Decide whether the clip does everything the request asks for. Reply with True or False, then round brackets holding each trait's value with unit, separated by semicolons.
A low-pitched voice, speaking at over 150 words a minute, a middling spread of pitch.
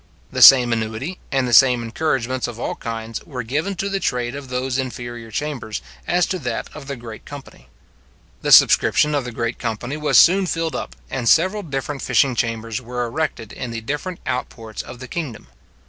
True (125 Hz; 195 wpm; 4.3 semitones)